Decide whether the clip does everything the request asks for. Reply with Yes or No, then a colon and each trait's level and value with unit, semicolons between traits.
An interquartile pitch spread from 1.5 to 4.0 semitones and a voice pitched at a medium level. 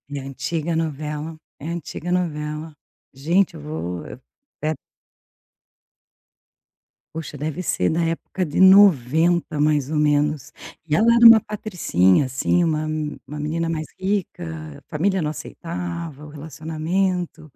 Yes: average, 2.8 semitones; medium, 155 Hz